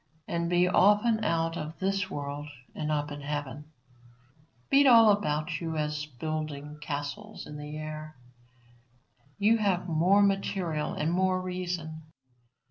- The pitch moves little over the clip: No, average, 4.4 semitones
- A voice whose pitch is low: No, medium, 165 Hz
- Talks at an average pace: No, slow, 130 wpm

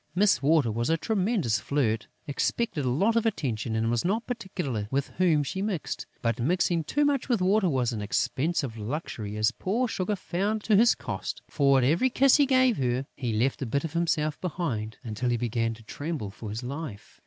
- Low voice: No, medium, 145 Hz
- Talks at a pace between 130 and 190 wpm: No, average, 200 wpm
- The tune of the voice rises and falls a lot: Yes, wide, 8.6 semitones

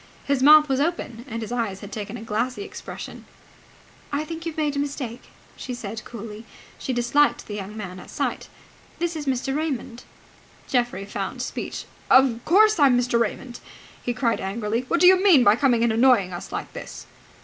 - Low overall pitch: No, high, 245 Hz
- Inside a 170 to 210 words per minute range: Yes, average, 190 wpm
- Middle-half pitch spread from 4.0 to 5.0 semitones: Yes, average, 4.4 semitones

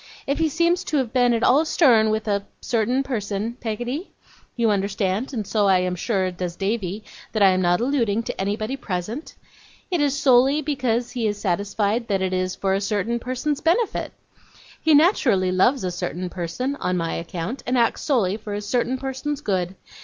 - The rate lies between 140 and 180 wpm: No, average, 190 wpm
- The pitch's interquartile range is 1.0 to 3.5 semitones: No, average, 5.3 semitones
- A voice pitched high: Yes, high, 220 Hz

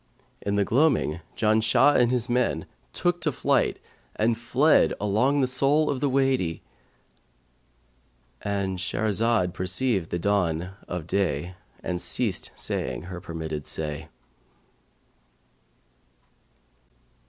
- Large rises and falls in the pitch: Yes, wide, 7.2 semitones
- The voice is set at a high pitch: No, low, 100 Hz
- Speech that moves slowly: Yes, slow, 105 wpm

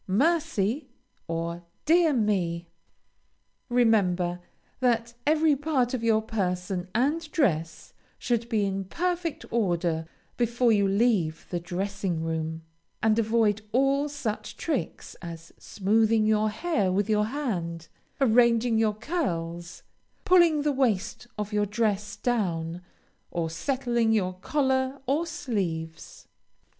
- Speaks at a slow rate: Yes, slow, 115 wpm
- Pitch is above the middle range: Yes, high, 215 Hz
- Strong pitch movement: Yes, wide, 6.1 semitones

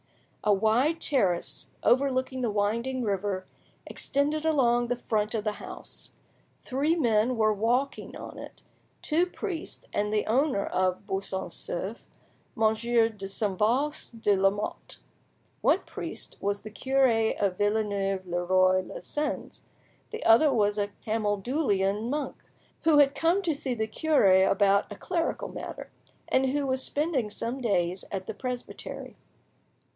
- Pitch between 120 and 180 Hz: No, high, 225 Hz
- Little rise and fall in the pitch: No, average, 5.0 semitones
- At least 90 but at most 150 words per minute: Yes, average, 140 wpm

